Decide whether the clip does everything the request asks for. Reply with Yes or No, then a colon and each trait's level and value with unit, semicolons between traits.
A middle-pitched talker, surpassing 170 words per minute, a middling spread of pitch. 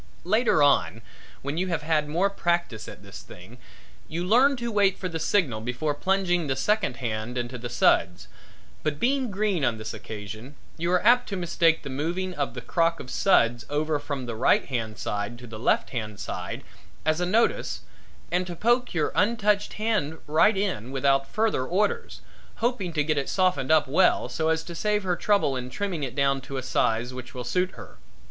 No: medium, 155 Hz; average, 195 wpm; wide, 7.0 semitones